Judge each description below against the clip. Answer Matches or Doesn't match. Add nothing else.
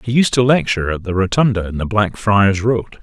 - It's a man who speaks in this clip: Matches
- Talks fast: Matches